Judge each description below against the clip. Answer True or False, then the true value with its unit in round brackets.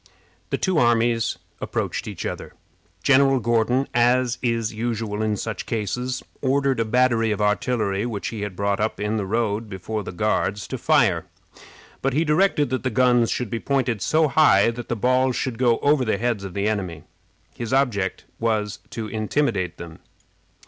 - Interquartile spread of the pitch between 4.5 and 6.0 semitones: False (3.5 semitones)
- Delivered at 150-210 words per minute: True (175 wpm)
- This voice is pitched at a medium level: False (115 Hz)